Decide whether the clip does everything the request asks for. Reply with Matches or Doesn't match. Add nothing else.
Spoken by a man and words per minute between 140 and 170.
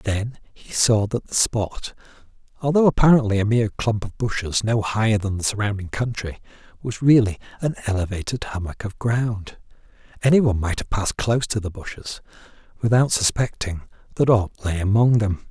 Matches